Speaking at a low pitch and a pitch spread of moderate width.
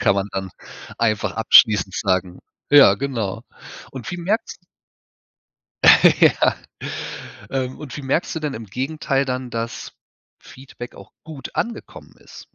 Yes: low, 125 Hz; average, 4.6 semitones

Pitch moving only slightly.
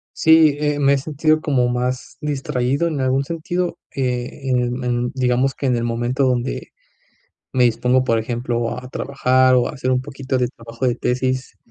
Yes: narrow, 2.2 semitones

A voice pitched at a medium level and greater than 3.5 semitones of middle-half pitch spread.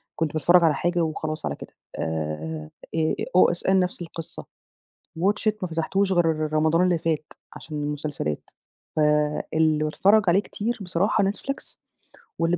No: medium, 165 Hz; average, 3.1 semitones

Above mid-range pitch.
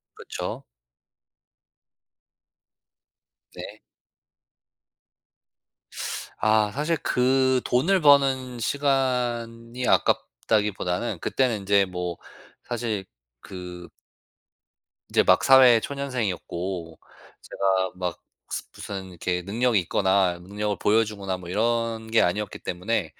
No: low, 110 Hz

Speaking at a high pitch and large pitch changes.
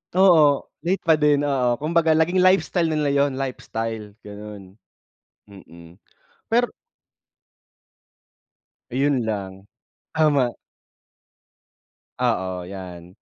No: low, 130 Hz; wide, 7.4 semitones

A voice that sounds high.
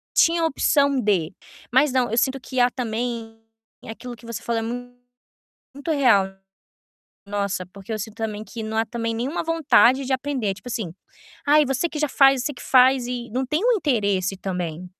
Yes: high, 245 Hz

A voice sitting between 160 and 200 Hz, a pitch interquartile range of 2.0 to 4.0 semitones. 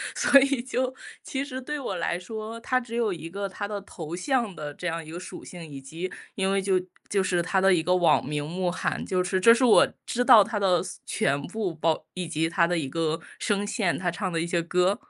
No: medium, 185 Hz; average, 4.4 semitones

